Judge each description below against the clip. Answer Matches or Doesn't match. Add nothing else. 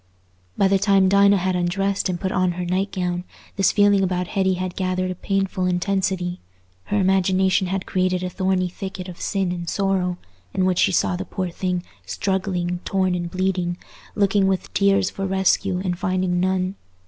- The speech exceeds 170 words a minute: Matches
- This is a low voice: Doesn't match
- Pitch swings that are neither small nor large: Doesn't match